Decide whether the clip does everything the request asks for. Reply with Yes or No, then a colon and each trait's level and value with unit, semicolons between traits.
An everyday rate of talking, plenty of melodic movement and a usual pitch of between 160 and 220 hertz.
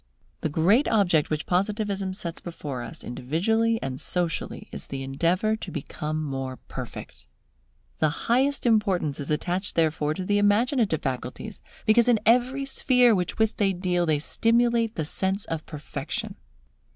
Yes: average, 150 wpm; wide, 6.3 semitones; medium, 185 Hz